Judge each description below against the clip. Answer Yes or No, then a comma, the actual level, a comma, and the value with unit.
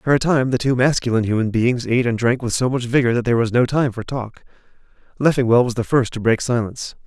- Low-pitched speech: Yes, low, 120 Hz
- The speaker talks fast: Yes, fast, 245 wpm